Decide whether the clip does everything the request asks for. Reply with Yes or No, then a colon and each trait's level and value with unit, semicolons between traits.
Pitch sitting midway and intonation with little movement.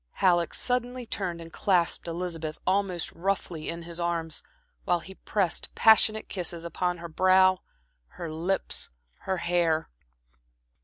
Yes: medium, 175 Hz; narrow, 2.1 semitones